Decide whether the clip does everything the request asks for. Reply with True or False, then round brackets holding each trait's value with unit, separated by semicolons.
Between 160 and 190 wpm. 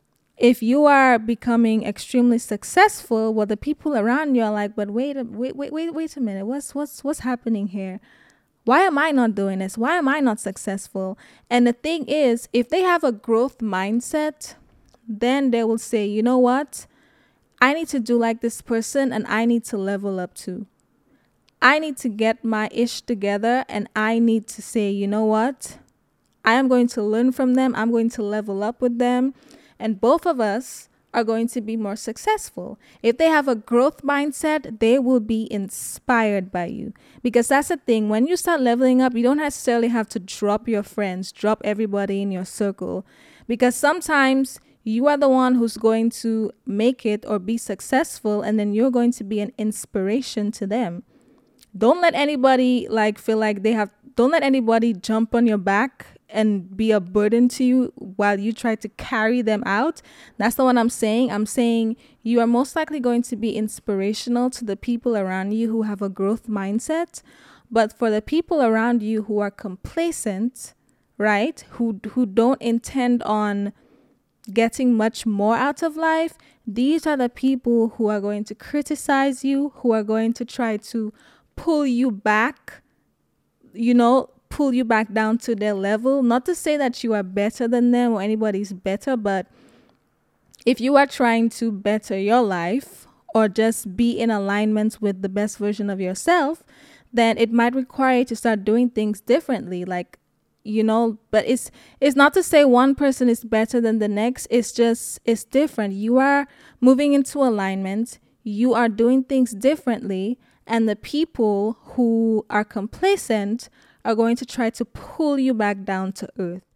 True (180 wpm)